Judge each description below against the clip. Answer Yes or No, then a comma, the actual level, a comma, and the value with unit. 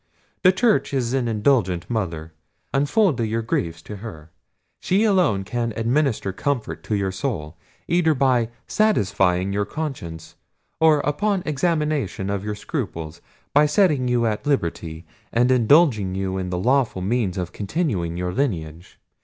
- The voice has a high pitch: No, low, 115 Hz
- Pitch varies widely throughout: Yes, wide, 7.3 semitones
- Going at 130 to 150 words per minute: Yes, average, 145 wpm